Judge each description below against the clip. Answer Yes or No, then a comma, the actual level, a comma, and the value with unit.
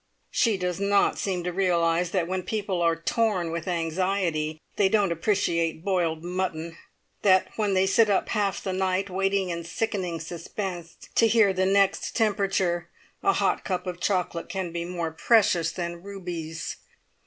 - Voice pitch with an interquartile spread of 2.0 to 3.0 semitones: Yes, average, 2.7 semitones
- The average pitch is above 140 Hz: Yes, medium, 185 Hz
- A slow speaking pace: No, average, 165 wpm